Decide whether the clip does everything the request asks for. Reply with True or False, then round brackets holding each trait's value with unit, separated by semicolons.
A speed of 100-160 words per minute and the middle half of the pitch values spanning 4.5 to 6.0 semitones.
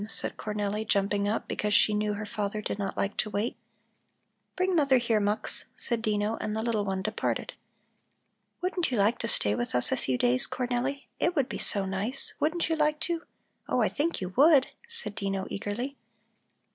False (190 wpm; 5.3 semitones)